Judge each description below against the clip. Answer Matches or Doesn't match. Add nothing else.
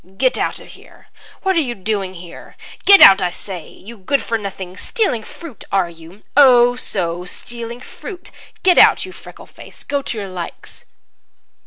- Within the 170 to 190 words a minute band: Matches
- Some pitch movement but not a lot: Doesn't match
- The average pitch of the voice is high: Matches